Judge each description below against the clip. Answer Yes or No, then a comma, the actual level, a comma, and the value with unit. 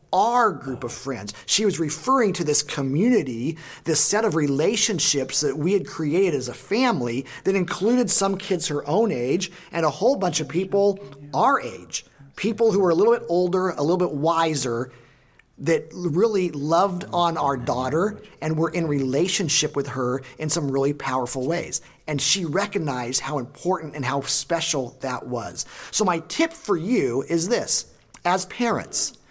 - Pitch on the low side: No, medium, 165 Hz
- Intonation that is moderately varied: No, wide, 5.7 semitones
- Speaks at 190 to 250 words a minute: No, average, 170 wpm